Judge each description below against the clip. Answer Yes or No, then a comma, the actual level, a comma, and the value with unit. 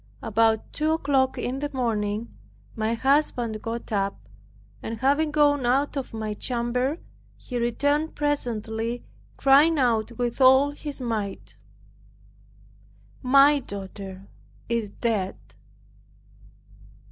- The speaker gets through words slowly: Yes, slow, 105 wpm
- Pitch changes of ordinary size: Yes, average, 4.1 semitones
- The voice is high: Yes, high, 245 Hz